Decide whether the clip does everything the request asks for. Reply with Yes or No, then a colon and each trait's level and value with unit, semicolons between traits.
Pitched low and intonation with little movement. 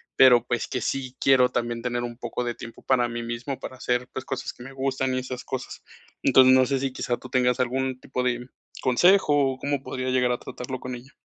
Yes: low, 125 Hz; narrow, 1.3 semitones